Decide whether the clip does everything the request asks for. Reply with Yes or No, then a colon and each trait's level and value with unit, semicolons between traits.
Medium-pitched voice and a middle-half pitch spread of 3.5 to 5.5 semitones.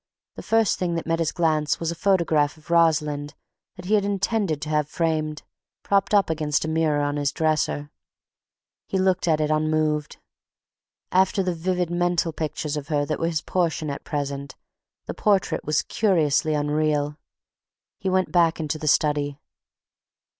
No: medium, 155 Hz; average, 2.7 semitones